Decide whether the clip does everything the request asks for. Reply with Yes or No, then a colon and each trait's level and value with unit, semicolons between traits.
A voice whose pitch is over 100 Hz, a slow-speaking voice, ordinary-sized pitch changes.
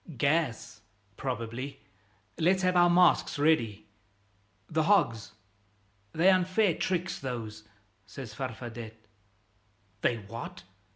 No: low, 135 Hz; slow, 95 wpm; wide, 7.4 semitones